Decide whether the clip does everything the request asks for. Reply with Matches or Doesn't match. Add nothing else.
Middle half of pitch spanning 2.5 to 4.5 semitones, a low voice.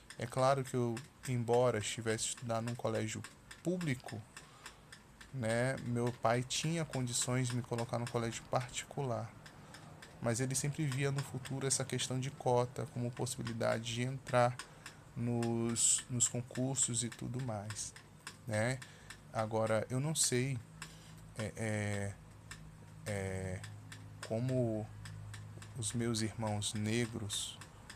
Matches